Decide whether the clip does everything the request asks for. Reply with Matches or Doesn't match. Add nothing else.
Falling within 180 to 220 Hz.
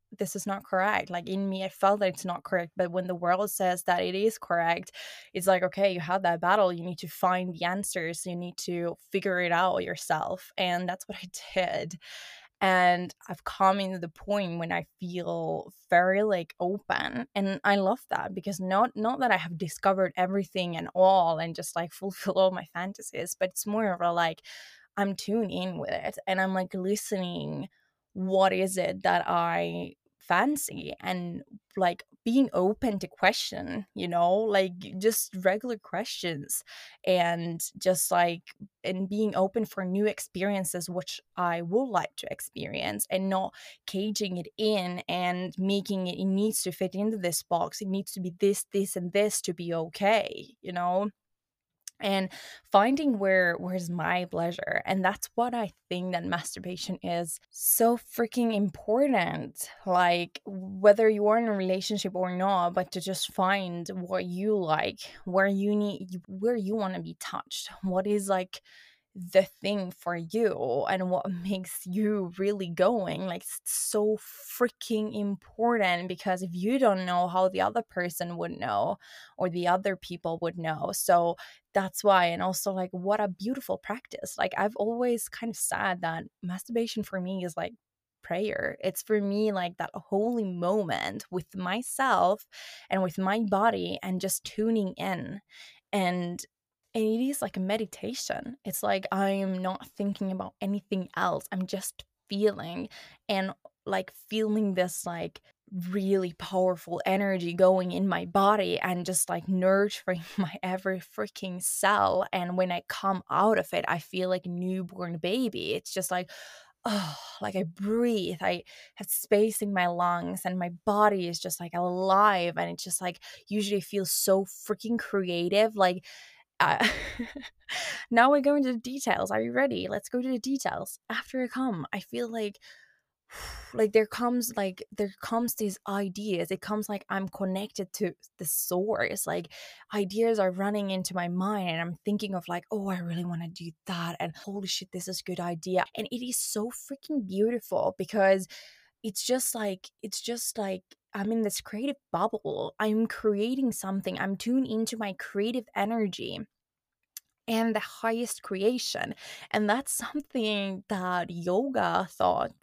Matches